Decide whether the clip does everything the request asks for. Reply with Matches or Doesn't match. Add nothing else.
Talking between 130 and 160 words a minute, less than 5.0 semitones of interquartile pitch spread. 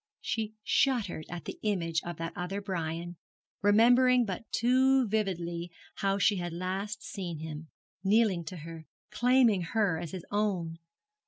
Matches